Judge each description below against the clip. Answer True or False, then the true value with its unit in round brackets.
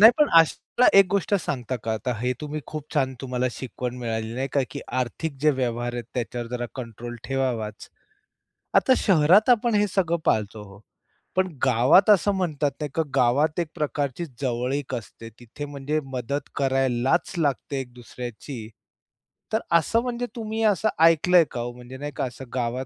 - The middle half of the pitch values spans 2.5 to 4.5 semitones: False (5.1 semitones)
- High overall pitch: False (135 Hz)